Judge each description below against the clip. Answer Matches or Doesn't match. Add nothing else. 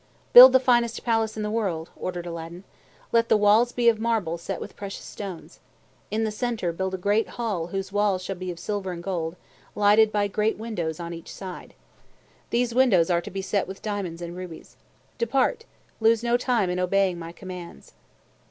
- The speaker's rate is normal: Matches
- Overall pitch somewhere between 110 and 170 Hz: Doesn't match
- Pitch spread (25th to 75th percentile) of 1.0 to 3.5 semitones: Doesn't match